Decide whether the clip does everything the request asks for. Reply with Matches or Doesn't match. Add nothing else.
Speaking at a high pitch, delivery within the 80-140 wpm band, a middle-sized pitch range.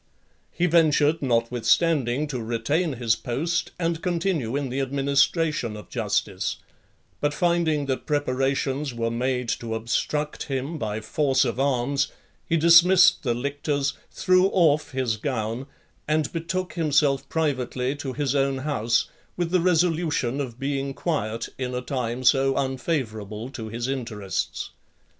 Doesn't match